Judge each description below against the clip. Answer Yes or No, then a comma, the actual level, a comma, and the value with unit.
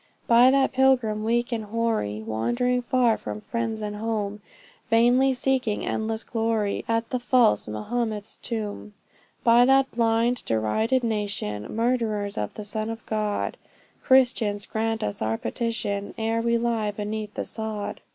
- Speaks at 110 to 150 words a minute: Yes, average, 140 wpm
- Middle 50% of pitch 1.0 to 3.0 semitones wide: Yes, narrow, 2.4 semitones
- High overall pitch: Yes, high, 225 Hz